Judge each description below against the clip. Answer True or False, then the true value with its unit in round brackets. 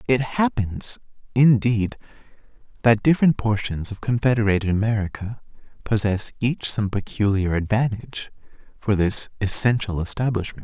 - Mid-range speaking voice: False (110 Hz)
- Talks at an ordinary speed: False (100 wpm)